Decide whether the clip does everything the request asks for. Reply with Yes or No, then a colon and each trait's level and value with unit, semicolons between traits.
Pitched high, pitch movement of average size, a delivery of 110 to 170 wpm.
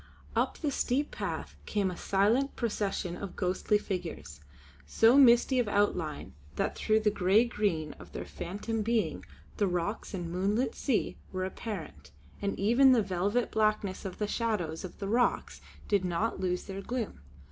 Yes: high, 205 Hz; average, 3.8 semitones; average, 160 wpm